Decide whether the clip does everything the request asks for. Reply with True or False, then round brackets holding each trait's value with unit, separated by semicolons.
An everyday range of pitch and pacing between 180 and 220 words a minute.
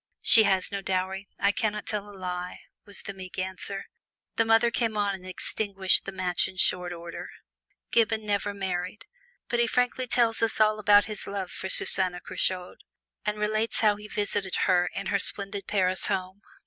False (2.3 semitones; 185 wpm)